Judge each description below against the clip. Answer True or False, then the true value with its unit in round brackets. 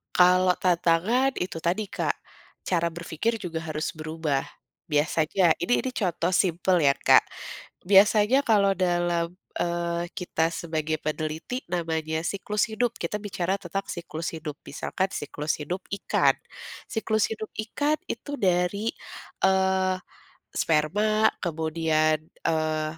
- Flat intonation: False (3.7 semitones)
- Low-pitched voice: False (175 Hz)